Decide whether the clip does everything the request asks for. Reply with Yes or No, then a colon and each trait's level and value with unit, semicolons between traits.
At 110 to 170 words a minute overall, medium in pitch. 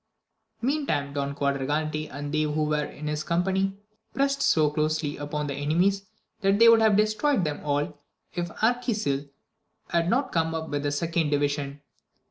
Yes: average, 165 wpm; medium, 155 Hz